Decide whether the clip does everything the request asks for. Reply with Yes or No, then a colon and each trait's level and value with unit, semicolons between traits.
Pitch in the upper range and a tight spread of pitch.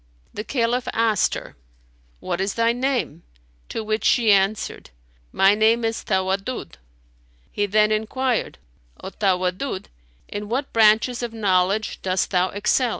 No: high, 215 Hz; average, 3.2 semitones